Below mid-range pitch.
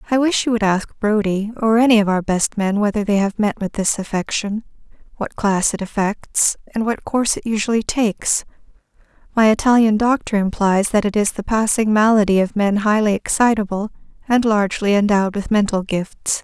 No: high, 210 Hz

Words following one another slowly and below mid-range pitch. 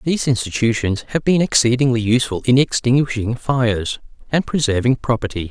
Yes: slow, 130 wpm; low, 125 Hz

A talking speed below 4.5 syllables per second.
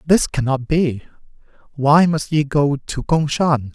Yes: 3.8 syllables/s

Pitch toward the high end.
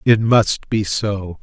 No: low, 105 Hz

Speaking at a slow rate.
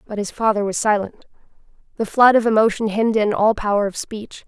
No: average, 200 wpm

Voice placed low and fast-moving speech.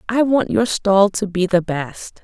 No: high, 200 Hz; fast, 215 wpm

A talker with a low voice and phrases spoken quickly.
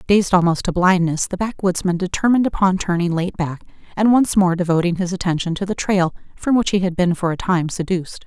No: medium, 180 Hz; fast, 210 wpm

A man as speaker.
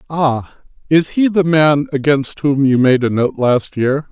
Yes: male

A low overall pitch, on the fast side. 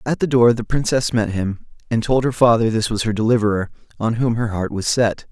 Yes: low, 115 Hz; fast, 235 wpm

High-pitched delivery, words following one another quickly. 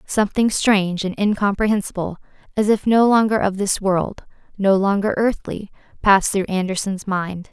No: high, 200 Hz; average, 145 wpm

